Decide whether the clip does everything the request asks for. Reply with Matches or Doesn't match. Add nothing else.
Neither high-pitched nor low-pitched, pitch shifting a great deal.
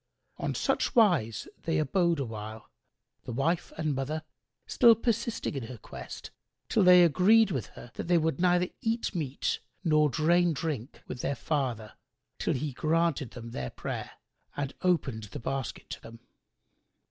Matches